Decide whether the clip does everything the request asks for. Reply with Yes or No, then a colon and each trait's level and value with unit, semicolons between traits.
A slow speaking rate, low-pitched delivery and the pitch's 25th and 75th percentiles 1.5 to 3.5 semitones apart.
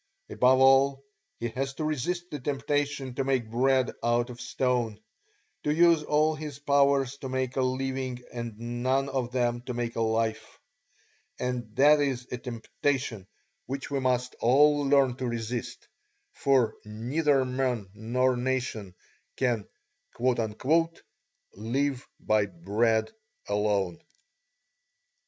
Yes: slow, 125 wpm; low, 130 Hz; narrow, 2.6 semitones